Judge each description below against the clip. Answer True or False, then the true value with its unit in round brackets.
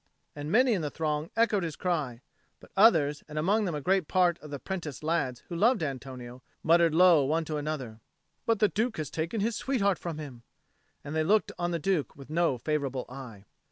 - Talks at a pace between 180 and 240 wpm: True (205 wpm)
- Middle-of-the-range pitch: True (160 Hz)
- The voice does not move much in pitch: False (4.5 semitones)